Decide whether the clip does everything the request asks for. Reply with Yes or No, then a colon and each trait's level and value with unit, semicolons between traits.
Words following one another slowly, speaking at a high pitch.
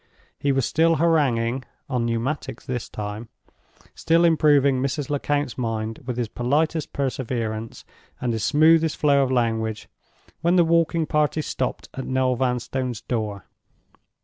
No: slow, 130 wpm; low, 130 Hz